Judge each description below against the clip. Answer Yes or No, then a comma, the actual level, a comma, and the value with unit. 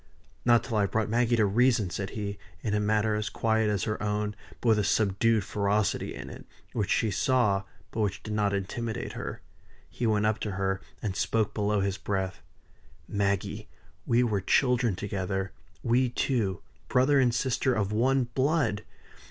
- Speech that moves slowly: No, average, 175 wpm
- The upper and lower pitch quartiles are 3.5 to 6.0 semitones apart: No, average, 2.8 semitones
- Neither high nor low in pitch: No, low, 105 Hz